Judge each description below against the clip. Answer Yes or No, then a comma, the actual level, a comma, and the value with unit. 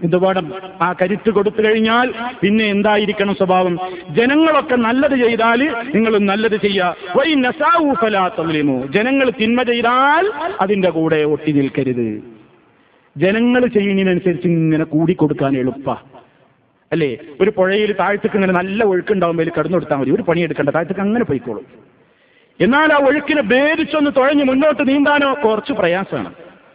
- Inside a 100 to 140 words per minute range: Yes, fast, 125 wpm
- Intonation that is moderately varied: No, wide, 6.4 semitones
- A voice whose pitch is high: Yes, high, 205 Hz